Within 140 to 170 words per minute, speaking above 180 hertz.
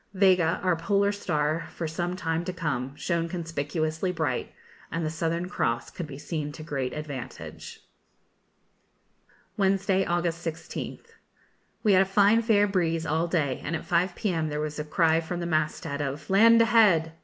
No: average, 165 wpm; medium, 165 Hz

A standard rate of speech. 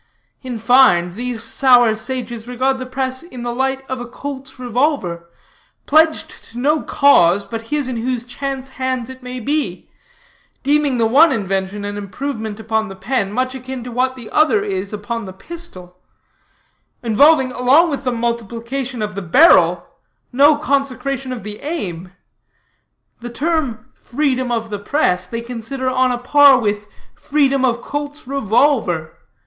Yes: average, 155 wpm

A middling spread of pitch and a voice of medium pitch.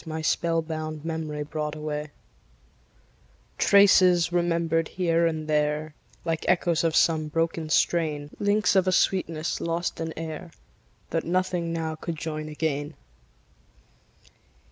No: narrow, 1.7 semitones; medium, 165 Hz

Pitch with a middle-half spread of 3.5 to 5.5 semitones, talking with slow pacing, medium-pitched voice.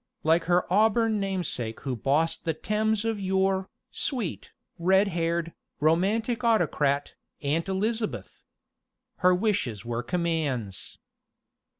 Yes: average, 4.9 semitones; slow, 105 wpm; medium, 180 Hz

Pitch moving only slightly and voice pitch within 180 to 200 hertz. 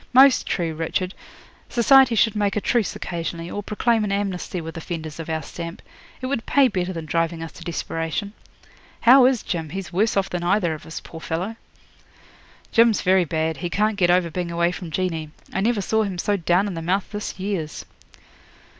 No: average, 3.9 semitones; medium, 185 Hz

